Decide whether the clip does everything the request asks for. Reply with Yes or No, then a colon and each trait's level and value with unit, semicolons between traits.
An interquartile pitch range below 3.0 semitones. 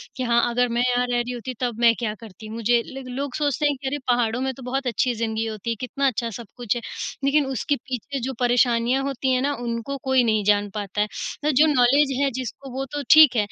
Yes: narrow, 2.5 semitones